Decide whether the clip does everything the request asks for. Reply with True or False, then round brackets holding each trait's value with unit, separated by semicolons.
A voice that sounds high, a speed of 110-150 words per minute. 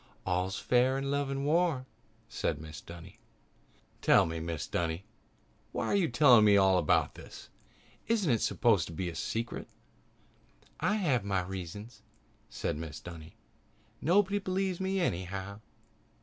False (105 Hz; 145 wpm)